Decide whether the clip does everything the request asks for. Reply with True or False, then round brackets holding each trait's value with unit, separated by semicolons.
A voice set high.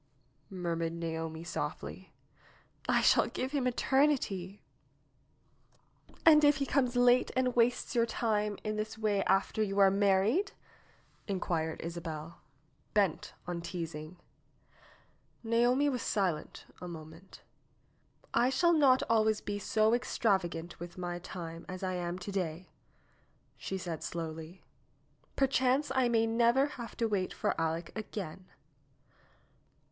True (200 Hz)